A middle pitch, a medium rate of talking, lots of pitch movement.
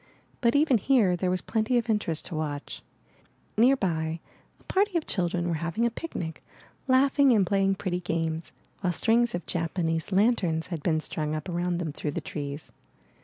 Yes: medium, 180 Hz; average, 170 wpm; wide, 6.1 semitones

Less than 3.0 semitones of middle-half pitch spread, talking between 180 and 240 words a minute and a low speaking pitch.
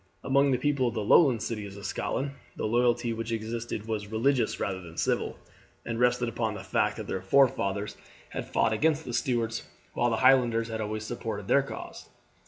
Yes: narrow, 2.4 semitones; average, 190 wpm; low, 115 Hz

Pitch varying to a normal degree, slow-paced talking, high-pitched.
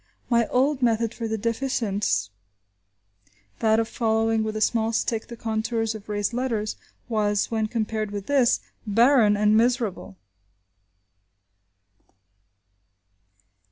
No: narrow, 1.7 semitones; slow, 115 wpm; high, 225 Hz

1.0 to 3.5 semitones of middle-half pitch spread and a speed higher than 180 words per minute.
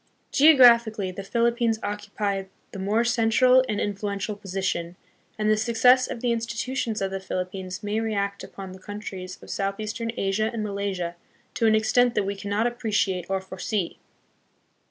No: average, 2.9 semitones; average, 155 wpm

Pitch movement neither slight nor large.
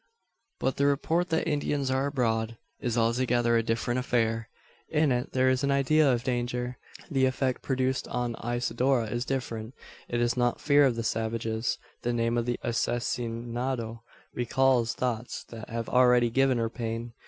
No: narrow, 2.2 semitones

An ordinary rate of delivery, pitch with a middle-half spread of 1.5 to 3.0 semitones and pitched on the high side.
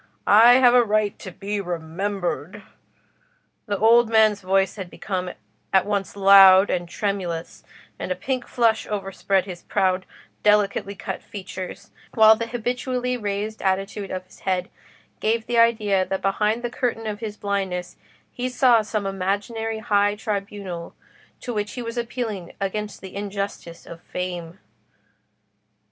Yes: average, 145 wpm; narrow, 2.6 semitones; high, 205 Hz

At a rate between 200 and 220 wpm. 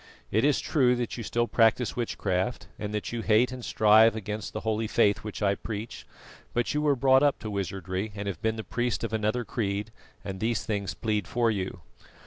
Yes: fast, 205 wpm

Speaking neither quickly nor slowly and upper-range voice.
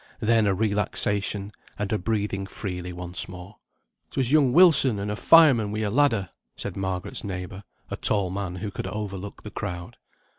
No: average, 170 wpm; low, 100 Hz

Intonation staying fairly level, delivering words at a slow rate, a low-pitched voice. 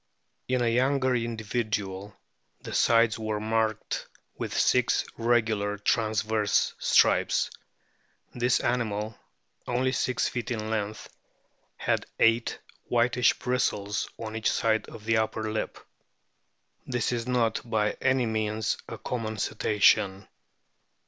Yes: narrow, 2.0 semitones; slow, 115 wpm; low, 110 Hz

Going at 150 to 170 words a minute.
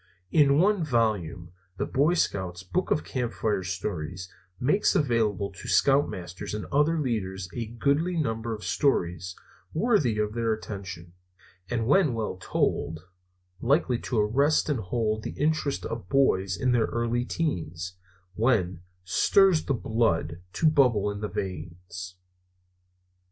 No: slow, 135 wpm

